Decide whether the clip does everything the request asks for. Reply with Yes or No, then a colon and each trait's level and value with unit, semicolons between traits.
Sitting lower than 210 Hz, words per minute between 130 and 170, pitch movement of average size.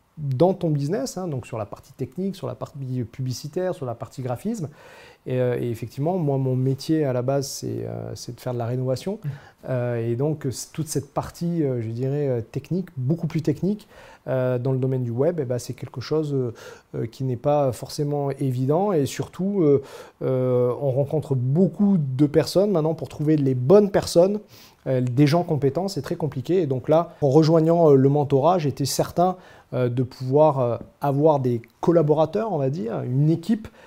Yes: medium, 140 Hz; average, 165 wpm; average, 4.0 semitones